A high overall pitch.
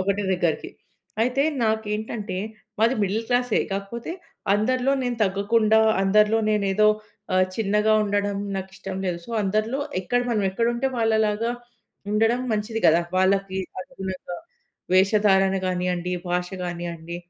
Yes: high, 205 Hz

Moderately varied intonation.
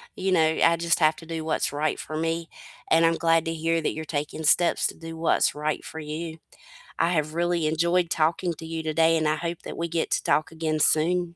No: narrow, 1.2 semitones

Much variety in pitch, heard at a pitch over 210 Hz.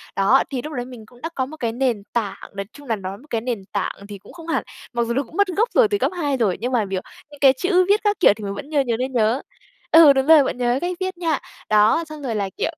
Yes: wide, 6.2 semitones; very high, 255 Hz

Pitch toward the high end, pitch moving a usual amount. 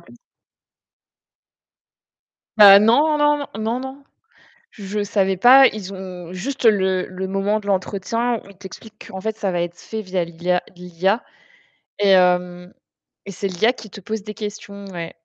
Yes: high, 200 Hz; average, 3.1 semitones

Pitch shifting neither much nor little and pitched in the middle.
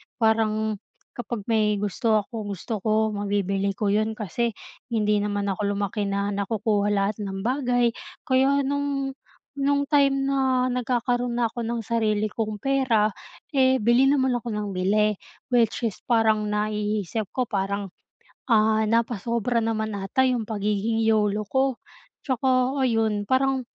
No: average, 3.1 semitones; high, 220 Hz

